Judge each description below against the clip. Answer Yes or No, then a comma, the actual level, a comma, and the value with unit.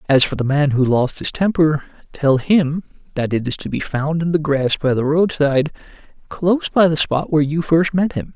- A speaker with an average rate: No, fast, 225 wpm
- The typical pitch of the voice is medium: Yes, medium, 150 Hz